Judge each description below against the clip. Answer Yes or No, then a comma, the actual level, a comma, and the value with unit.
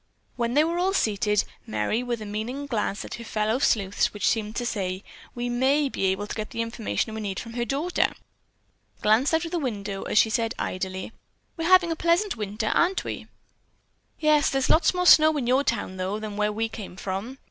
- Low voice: No, high, 230 Hz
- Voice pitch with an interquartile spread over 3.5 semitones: Yes, wide, 5.4 semitones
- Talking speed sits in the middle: No, fast, 210 wpm